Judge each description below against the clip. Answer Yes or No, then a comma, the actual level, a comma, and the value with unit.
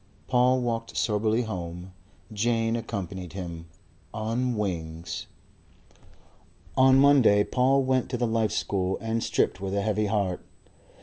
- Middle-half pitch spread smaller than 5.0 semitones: Yes, average, 4.2 semitones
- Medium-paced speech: No, slow, 125 wpm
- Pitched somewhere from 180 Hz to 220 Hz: No, low, 110 Hz